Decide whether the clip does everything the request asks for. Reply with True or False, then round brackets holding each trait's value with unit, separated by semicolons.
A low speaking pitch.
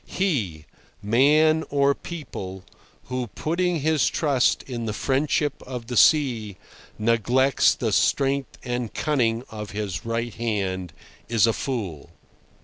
True (120 Hz)